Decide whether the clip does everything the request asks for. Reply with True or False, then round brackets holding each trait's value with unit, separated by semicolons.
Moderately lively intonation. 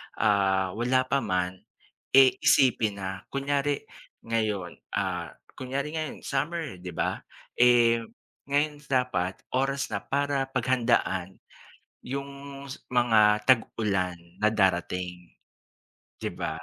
False (6.1 semitones)